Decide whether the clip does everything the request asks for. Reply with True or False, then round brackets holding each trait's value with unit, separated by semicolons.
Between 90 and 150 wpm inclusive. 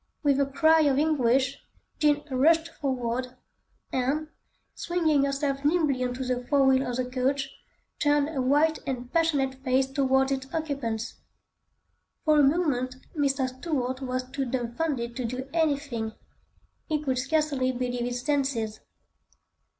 True (140 wpm)